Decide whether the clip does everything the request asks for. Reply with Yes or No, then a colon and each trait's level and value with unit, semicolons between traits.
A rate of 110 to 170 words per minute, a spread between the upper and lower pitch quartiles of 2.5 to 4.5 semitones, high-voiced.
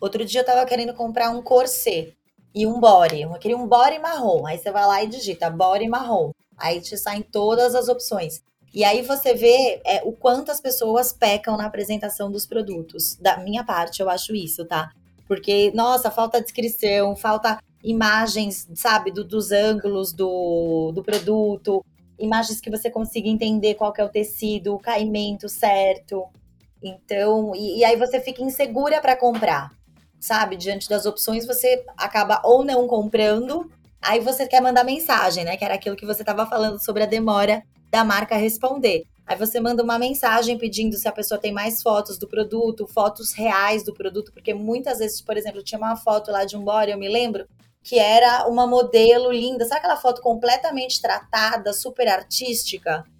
No: average, 180 wpm; average, 2.8 semitones; high, 215 Hz